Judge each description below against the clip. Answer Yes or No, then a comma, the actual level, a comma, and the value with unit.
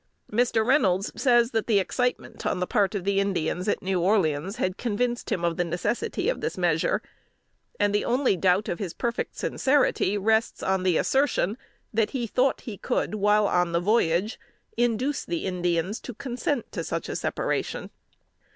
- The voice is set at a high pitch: Yes, high, 205 Hz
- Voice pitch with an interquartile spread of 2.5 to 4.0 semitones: No, average, 4.8 semitones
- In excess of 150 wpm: Yes, average, 170 wpm